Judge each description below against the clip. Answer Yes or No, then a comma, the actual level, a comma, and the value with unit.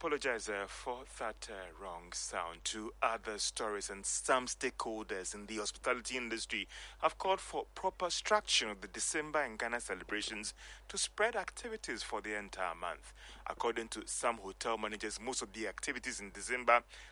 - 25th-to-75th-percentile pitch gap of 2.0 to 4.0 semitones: No, average, 5.2 semitones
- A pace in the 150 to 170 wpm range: Yes, average, 160 wpm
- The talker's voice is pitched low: Yes, low, 115 Hz